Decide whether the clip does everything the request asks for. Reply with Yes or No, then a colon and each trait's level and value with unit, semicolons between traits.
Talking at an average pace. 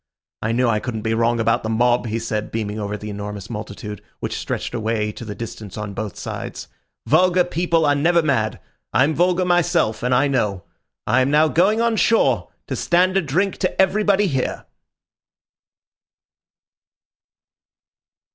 Yes: average, 160 wpm